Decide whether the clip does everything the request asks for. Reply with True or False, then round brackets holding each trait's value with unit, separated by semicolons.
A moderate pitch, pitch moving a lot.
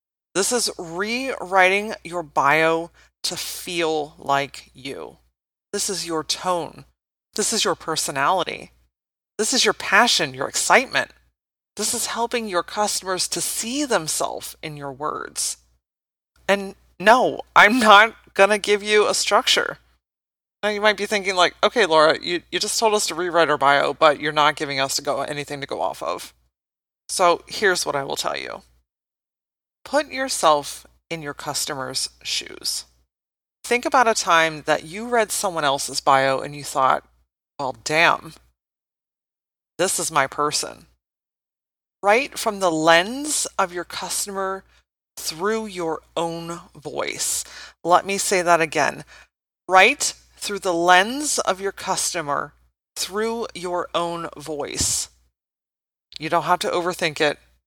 True (170 Hz; 6.1 semitones)